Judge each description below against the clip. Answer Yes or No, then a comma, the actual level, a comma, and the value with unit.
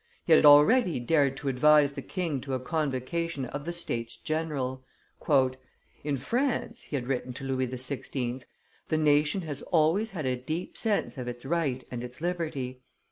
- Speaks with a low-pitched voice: No, medium, 145 Hz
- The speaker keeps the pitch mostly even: No, average, 4.1 semitones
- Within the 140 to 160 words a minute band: No, average, 170 wpm